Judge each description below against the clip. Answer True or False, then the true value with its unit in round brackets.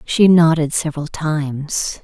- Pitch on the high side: False (155 Hz)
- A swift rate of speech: False (120 wpm)